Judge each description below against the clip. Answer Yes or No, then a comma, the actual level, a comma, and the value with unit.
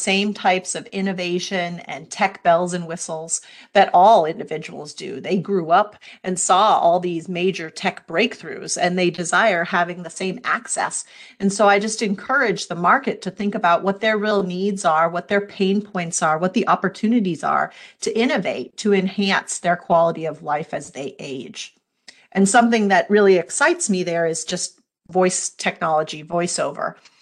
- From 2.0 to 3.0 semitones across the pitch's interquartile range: Yes, average, 2.7 semitones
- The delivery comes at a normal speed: Yes, average, 170 wpm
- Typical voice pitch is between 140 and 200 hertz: Yes, medium, 185 Hz